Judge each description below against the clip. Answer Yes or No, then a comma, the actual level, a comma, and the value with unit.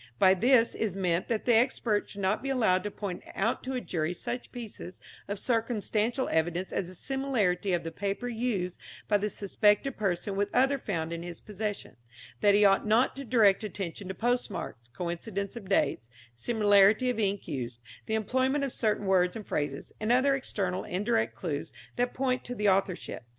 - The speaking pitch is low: No, high, 205 Hz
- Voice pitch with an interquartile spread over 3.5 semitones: Yes, average, 4.5 semitones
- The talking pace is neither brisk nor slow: Yes, average, 185 wpm